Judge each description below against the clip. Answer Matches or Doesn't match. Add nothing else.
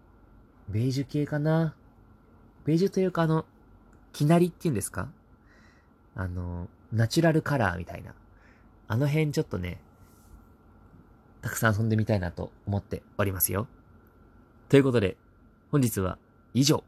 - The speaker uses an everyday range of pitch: Doesn't match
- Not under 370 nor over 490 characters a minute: Doesn't match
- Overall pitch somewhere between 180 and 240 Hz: Doesn't match